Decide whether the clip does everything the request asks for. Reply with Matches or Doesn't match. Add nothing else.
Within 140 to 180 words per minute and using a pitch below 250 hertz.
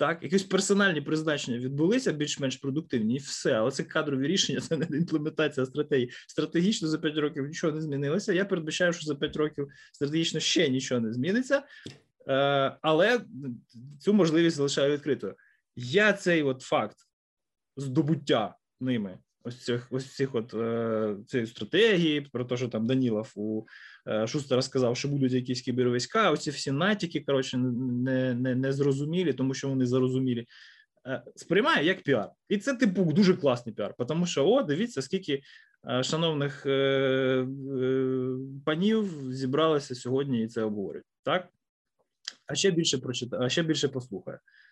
Matches